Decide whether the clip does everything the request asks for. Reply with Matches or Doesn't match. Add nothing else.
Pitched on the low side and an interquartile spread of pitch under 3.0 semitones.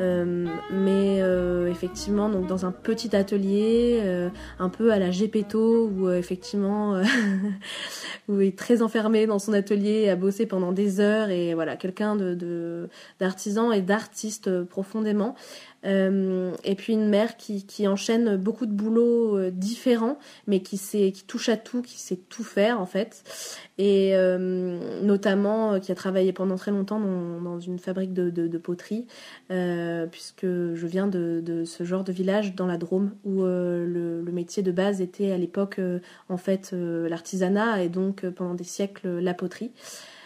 Doesn't match